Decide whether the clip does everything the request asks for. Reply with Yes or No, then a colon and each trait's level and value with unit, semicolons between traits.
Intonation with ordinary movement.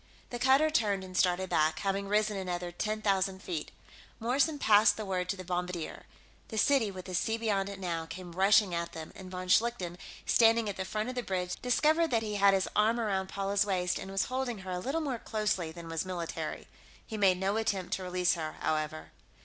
Yes: average, 3.3 semitones